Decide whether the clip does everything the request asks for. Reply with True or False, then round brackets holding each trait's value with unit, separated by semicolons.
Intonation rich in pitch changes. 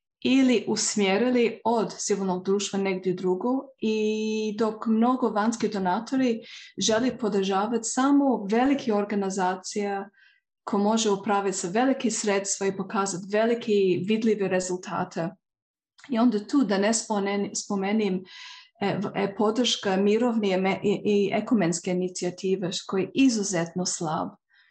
False (2.9 semitones)